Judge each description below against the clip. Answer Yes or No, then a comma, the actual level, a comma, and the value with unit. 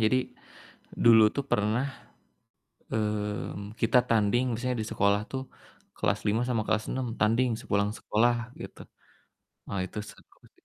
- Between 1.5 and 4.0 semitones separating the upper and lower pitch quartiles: Yes, average, 2.7 semitones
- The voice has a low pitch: Yes, low, 110 Hz